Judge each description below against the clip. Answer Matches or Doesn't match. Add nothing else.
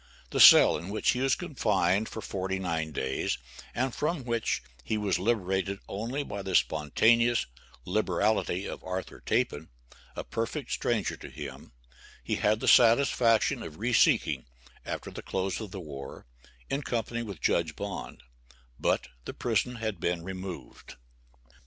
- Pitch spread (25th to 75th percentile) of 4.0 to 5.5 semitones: Matches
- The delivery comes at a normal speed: Matches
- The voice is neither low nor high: Doesn't match